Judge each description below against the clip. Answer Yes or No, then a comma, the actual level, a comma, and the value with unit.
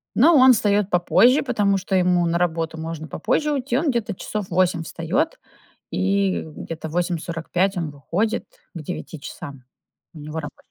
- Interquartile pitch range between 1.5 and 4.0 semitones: No, average, 4.4 semitones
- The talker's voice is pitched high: No, medium, 180 Hz